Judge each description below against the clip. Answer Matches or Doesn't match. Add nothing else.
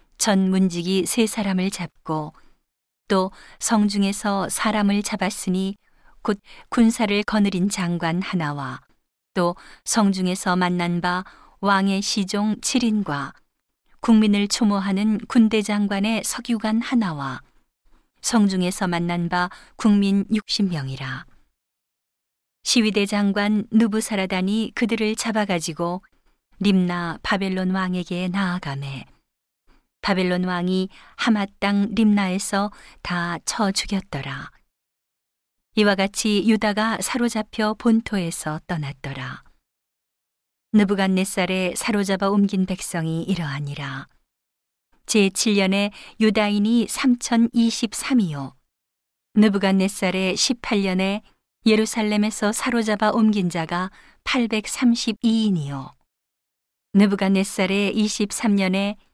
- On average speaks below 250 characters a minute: Matches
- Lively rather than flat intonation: Doesn't match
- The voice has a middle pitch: Doesn't match